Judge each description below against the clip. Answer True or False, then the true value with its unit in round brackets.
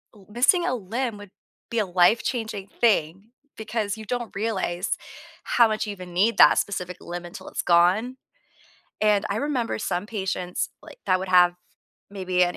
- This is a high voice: True (205 Hz)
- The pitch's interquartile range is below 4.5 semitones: True (3.9 semitones)